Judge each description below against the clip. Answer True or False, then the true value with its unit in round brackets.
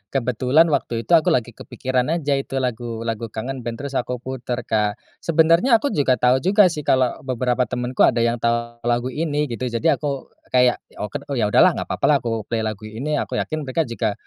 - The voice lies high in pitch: False (125 Hz)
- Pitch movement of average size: True (3.6 semitones)